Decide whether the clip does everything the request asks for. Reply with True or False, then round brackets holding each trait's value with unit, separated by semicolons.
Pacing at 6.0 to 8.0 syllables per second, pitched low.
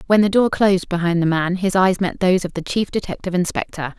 False (6.3 syllables/s; 185 Hz)